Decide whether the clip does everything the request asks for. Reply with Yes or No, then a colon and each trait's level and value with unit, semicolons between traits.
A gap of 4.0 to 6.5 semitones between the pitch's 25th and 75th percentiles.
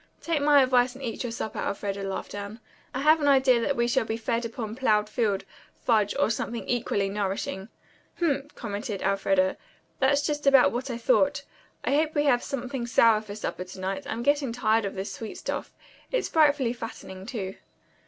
Yes: average, 4.9 semitones